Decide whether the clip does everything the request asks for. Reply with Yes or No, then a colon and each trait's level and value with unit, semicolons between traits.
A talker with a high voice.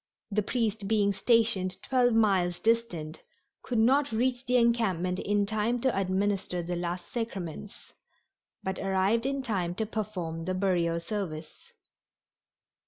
Yes: high, 200 Hz